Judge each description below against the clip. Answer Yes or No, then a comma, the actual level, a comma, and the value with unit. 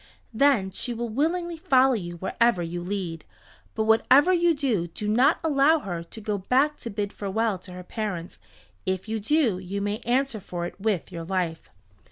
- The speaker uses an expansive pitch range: Yes, wide, 6.3 semitones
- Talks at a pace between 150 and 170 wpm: No, average, 185 wpm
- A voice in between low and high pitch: No, high, 215 Hz